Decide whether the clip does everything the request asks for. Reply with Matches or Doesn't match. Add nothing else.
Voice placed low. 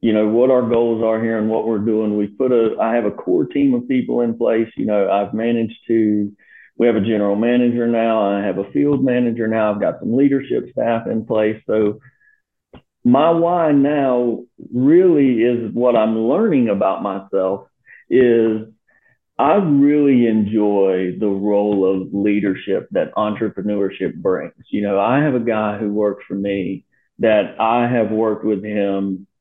Matches